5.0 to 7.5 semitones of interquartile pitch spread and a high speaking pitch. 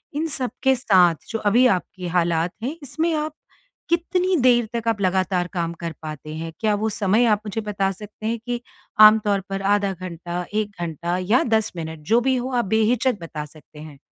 Yes: wide, 5.4 semitones; high, 205 Hz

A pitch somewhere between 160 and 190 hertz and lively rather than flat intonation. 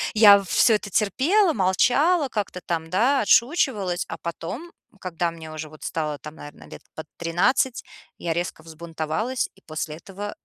Yes: medium, 185 Hz; wide, 6.7 semitones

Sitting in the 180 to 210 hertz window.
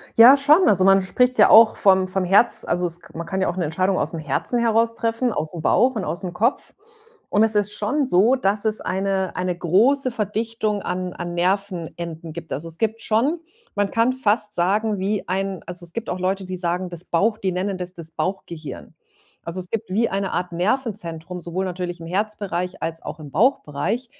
Yes: high, 190 Hz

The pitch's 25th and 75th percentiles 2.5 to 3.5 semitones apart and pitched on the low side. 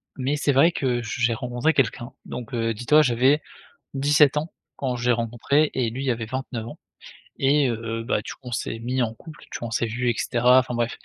Yes: average, 2.9 semitones; low, 125 Hz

